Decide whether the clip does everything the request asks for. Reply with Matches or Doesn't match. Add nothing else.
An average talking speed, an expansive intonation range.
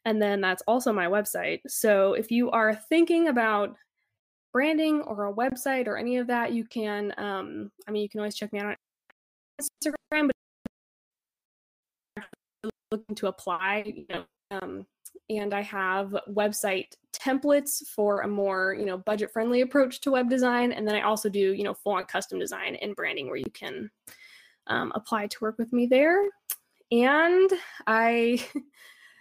Doesn't match